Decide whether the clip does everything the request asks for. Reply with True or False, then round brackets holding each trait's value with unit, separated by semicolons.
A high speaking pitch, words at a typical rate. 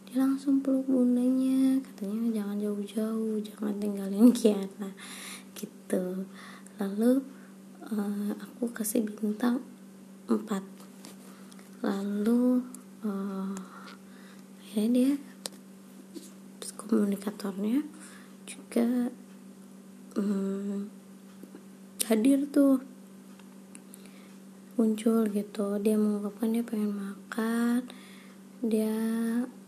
False (210 Hz; 70 wpm)